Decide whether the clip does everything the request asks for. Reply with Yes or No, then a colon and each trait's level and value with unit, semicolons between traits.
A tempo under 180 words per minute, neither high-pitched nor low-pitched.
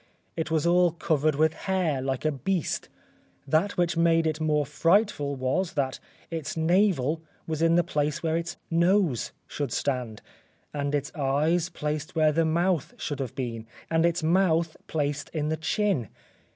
Yes: average, 165 wpm; medium, 160 Hz